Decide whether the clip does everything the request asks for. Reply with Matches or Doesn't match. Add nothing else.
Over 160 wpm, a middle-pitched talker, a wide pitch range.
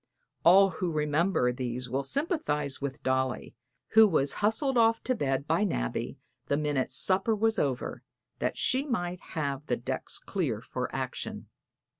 Doesn't match